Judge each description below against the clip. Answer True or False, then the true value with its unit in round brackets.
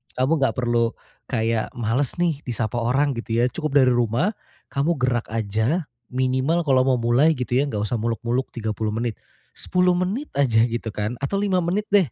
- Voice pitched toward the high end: False (125 Hz)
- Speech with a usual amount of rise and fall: True (4.5 semitones)